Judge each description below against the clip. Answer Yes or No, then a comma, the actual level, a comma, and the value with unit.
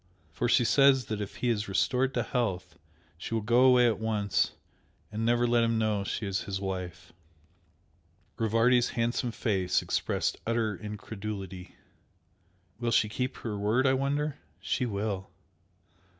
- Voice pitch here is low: Yes, low, 110 Hz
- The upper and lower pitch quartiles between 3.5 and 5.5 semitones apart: No, average, 3.1 semitones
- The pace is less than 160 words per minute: Yes, average, 150 wpm